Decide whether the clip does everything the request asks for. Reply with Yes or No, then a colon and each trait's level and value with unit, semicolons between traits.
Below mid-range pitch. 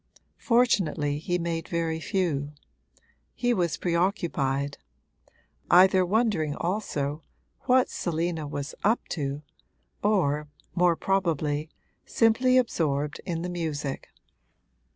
No: medium, 170 Hz